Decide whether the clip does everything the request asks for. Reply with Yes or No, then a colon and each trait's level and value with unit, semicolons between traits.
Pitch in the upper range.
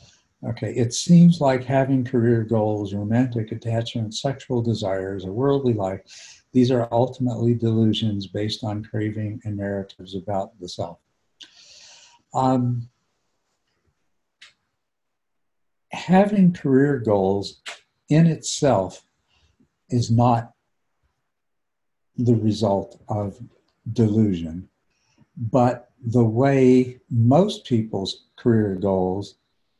No: low, 115 Hz